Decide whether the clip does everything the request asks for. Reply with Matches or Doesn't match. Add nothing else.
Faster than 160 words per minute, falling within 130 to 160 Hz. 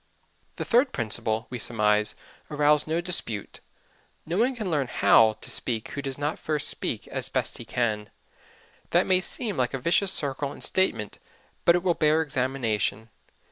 Matches